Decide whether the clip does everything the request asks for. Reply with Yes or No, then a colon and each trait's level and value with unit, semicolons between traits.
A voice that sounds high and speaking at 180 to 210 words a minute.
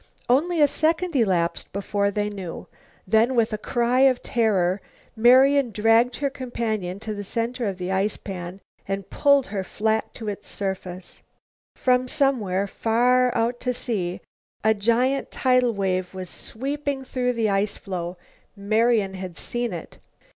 No: high, 220 Hz; average, 150 wpm